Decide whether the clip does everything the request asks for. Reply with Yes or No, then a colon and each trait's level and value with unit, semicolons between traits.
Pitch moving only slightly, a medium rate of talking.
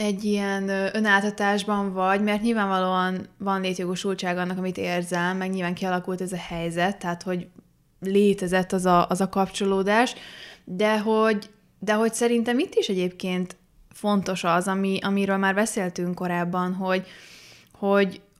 Yes: narrow, 1.9 semitones; average, 135 wpm